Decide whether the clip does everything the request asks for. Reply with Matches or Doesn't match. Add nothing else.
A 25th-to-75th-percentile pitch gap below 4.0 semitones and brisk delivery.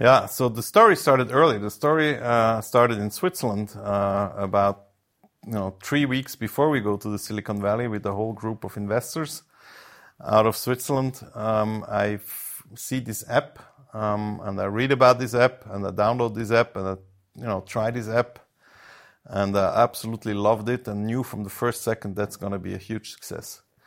Doesn't match